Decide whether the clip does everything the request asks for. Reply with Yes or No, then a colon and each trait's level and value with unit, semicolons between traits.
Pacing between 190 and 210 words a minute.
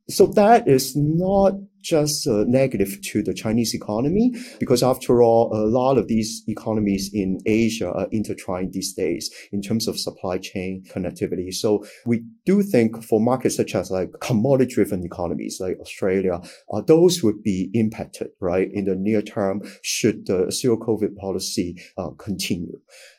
No: average, 155 wpm